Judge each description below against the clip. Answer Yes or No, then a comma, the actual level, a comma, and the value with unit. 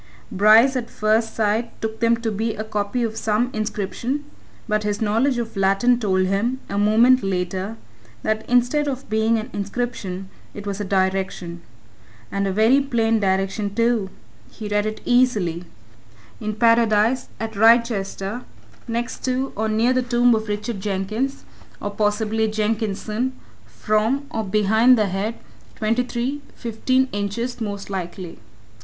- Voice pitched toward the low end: No, high, 220 Hz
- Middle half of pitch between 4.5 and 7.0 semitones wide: No, average, 2.8 semitones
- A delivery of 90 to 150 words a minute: Yes, average, 145 wpm